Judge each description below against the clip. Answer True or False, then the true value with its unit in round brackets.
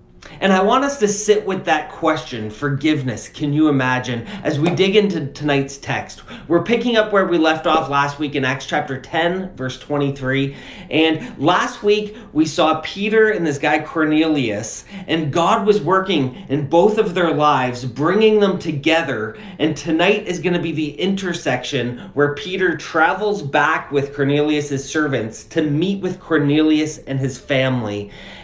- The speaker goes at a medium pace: True (165 wpm)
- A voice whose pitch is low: False (155 Hz)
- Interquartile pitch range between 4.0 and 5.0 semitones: True (4.6 semitones)